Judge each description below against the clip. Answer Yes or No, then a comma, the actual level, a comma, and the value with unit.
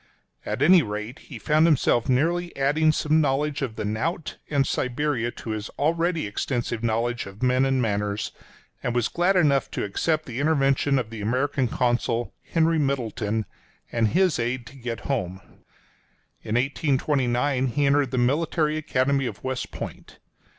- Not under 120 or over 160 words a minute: Yes, average, 155 wpm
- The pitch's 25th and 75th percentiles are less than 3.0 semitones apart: No, average, 4.2 semitones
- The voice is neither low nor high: No, low, 130 Hz